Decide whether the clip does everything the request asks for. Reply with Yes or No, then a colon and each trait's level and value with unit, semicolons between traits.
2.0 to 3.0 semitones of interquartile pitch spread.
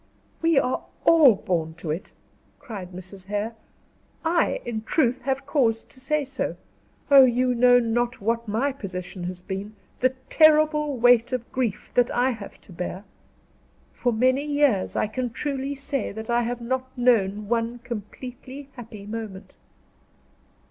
No: average, 3.9 semitones